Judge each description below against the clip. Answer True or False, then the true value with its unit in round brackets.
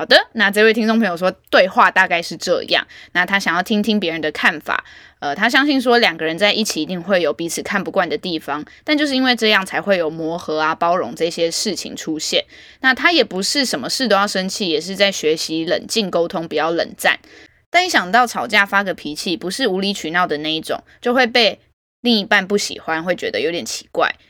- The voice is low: False (195 Hz)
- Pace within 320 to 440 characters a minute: True (330 characters per minute)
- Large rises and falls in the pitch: True (6.1 semitones)